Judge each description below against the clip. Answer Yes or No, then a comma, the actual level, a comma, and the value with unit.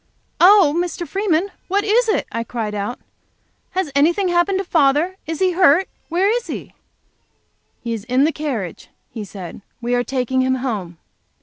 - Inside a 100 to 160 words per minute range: No, average, 170 wpm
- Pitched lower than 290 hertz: No, very high, 300 Hz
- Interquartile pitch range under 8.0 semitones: Yes, wide, 7.3 semitones